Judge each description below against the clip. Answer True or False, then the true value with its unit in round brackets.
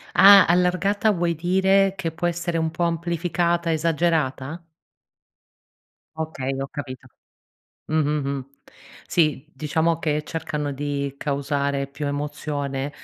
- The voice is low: False (155 Hz)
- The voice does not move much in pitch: False (3.3 semitones)